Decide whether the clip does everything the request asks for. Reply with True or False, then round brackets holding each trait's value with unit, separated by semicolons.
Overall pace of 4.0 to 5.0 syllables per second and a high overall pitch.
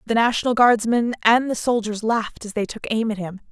False (5.8 syllables/s; 225 Hz)